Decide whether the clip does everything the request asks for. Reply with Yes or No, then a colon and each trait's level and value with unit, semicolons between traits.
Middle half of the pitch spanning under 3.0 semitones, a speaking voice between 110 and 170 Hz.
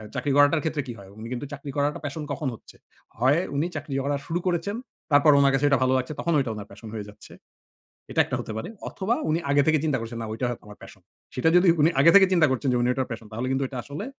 No: average, 4.1 semitones; medium, 140 Hz